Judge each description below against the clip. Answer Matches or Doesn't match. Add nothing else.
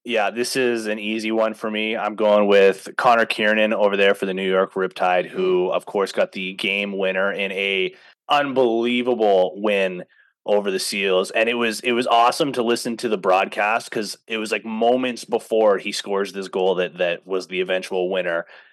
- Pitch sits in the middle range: Doesn't match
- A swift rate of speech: Doesn't match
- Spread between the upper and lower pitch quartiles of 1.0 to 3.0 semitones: Doesn't match